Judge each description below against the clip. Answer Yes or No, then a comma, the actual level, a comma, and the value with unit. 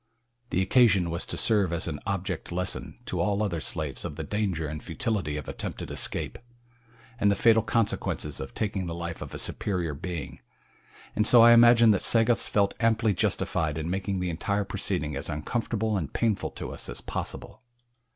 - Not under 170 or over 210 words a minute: Yes, average, 180 wpm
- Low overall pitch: Yes, very low, 95 Hz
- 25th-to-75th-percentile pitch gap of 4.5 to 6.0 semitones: Yes, average, 5.0 semitones